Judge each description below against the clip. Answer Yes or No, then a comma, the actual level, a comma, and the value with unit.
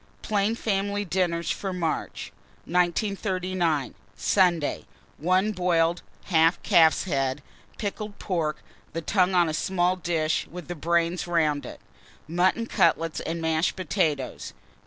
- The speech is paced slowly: Yes, slow, 120 wpm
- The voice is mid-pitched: Yes, medium, 175 Hz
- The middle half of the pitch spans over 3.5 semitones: No, narrow, 2.5 semitones